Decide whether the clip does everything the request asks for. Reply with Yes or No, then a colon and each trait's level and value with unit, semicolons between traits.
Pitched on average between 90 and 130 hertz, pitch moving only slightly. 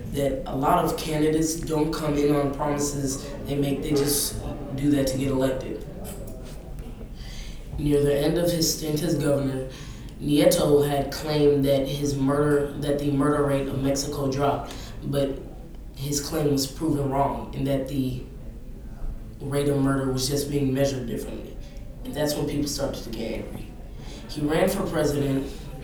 No: medium, 140 Hz; narrow, 1.3 semitones